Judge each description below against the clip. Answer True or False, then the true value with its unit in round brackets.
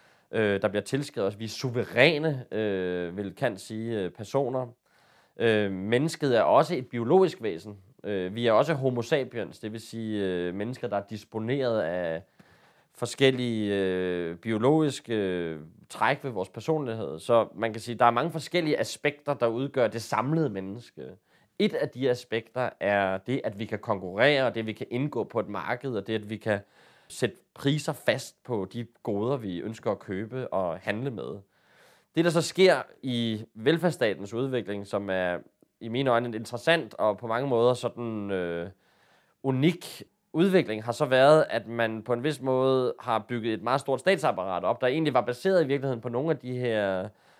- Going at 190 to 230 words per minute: False (180 wpm)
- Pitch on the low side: True (115 Hz)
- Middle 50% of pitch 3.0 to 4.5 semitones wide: True (4.2 semitones)